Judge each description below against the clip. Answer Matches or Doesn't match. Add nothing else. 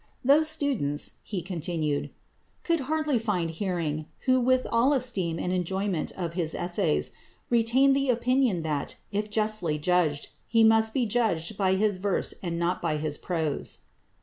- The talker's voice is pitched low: Doesn't match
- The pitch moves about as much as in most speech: Doesn't match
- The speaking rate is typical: Matches